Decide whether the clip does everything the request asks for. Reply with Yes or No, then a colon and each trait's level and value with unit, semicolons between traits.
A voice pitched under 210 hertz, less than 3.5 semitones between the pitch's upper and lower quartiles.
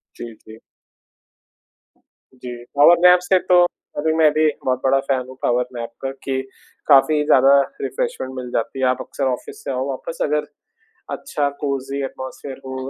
Yes: low, 135 Hz; narrow, 2.6 semitones